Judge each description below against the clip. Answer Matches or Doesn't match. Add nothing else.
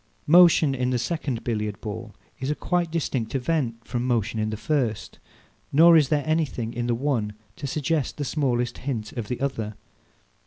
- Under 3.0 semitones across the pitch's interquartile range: Doesn't match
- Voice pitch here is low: Matches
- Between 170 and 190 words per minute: Matches